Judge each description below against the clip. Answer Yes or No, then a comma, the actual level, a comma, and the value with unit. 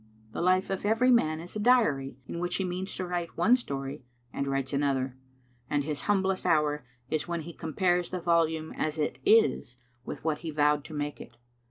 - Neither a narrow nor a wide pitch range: Yes, average, 3.9 semitones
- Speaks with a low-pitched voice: No, medium, 160 Hz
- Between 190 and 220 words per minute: Yes, average, 200 wpm